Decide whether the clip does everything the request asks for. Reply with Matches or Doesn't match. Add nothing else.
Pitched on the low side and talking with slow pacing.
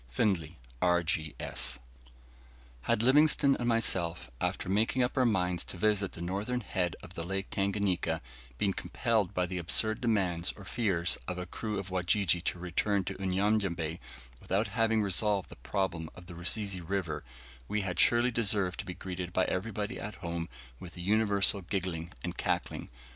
Doesn't match